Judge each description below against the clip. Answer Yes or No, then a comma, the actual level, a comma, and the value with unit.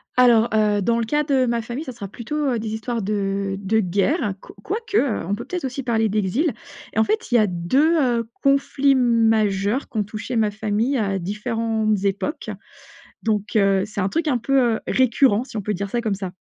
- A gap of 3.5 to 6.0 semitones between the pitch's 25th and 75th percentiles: Yes, average, 4.0 semitones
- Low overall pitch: No, high, 225 Hz